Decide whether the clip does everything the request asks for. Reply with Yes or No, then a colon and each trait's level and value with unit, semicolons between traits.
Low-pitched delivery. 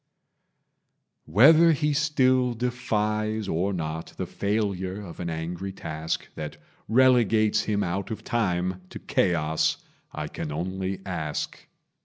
Yes: low, 100 Hz